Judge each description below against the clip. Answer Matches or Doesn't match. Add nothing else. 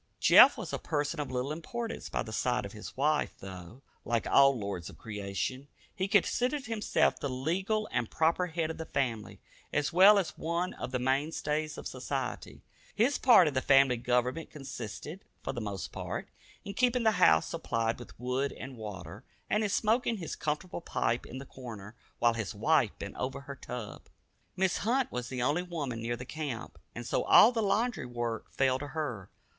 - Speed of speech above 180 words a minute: Matches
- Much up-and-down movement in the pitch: Matches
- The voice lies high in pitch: Doesn't match